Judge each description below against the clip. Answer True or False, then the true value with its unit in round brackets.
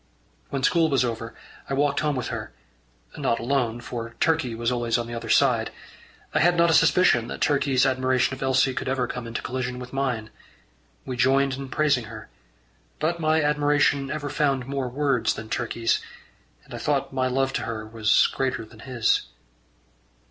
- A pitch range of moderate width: True (3.1 semitones)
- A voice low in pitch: True (130 Hz)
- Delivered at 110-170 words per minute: False (180 wpm)